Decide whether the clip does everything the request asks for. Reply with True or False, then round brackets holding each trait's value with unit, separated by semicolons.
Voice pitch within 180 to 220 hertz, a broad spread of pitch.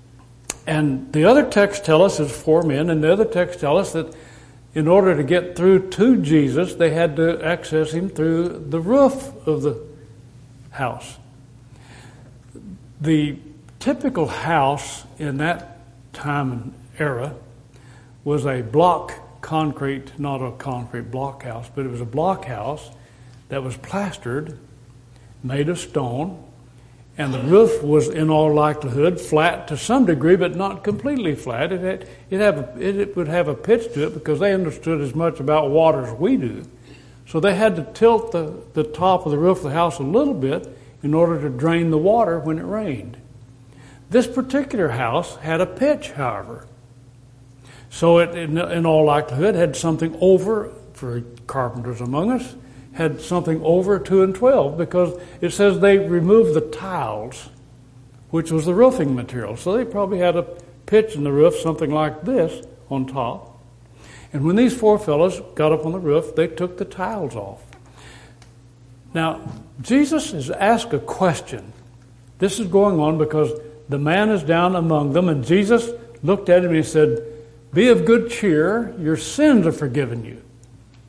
False (155 Hz; 5.9 semitones)